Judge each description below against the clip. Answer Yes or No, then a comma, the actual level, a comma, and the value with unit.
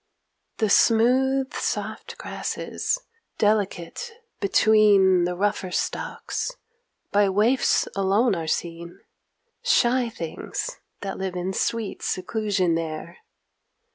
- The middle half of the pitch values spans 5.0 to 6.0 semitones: No, average, 4.2 semitones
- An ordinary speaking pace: No, slow, 95 wpm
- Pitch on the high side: Yes, high, 200 Hz